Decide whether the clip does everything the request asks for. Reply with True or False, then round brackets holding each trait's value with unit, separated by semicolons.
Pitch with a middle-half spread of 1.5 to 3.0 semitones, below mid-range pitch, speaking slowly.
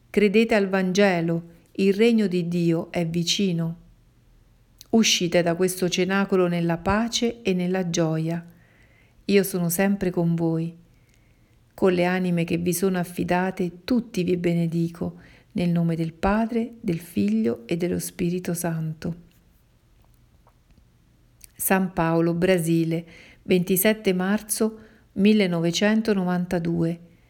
False (2.7 semitones; 175 Hz; 110 wpm)